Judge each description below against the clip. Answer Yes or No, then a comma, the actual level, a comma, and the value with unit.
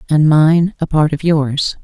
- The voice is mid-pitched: Yes, medium, 155 Hz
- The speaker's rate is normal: Yes, average, 195 wpm